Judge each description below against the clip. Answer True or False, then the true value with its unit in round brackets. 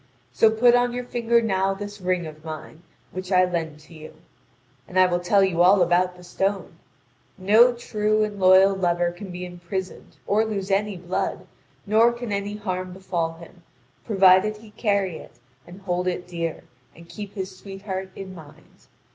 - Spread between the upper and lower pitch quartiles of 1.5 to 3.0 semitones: True (2.7 semitones)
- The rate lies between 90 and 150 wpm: False (175 wpm)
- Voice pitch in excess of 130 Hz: True (190 Hz)